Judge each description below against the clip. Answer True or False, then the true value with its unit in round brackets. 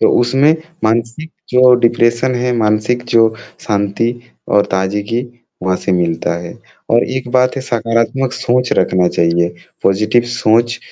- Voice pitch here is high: False (115 Hz)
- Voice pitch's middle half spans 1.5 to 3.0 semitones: False (3.4 semitones)